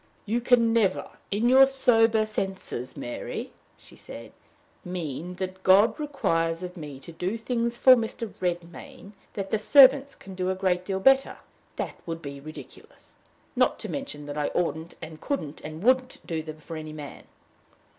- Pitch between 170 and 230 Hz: Yes, medium, 185 Hz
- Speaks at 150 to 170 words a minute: Yes, average, 165 wpm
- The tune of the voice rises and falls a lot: Yes, wide, 6.2 semitones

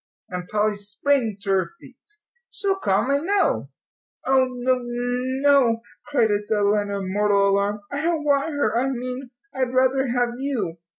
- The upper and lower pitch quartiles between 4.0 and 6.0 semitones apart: Yes, average, 4.7 semitones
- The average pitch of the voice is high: Yes, high, 245 Hz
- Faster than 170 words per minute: No, average, 155 wpm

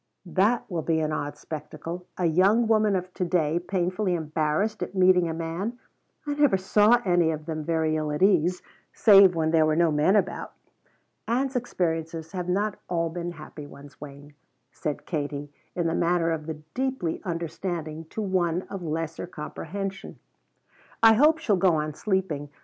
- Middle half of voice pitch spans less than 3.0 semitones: No, average, 3.5 semitones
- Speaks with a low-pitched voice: No, medium, 170 Hz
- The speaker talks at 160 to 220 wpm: Yes, average, 170 wpm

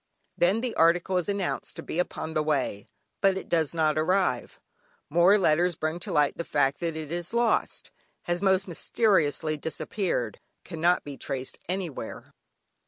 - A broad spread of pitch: No, average, 3.4 semitones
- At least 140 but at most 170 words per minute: Yes, average, 160 wpm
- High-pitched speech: No, medium, 170 Hz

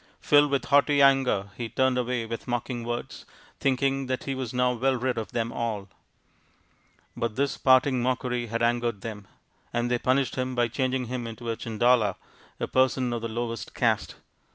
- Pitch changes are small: Yes, narrow, 2.0 semitones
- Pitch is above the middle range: No, low, 125 Hz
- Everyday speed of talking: Yes, average, 175 wpm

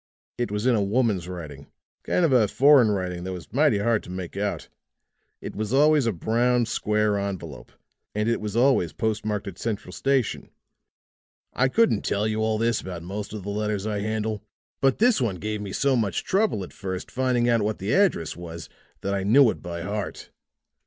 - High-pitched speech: No, low, 105 Hz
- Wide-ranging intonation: No, average, 3.6 semitones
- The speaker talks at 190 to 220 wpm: Yes, average, 200 wpm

